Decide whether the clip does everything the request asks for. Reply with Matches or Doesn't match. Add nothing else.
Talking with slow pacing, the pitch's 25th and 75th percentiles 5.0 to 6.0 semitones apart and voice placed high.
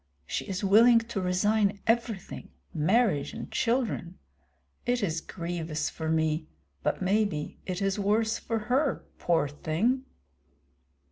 Matches